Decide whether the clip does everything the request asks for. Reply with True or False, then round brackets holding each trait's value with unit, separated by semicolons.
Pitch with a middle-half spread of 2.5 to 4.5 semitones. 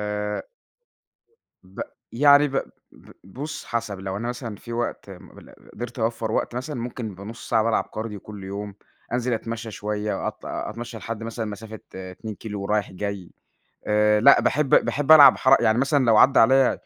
True (2.8 semitones)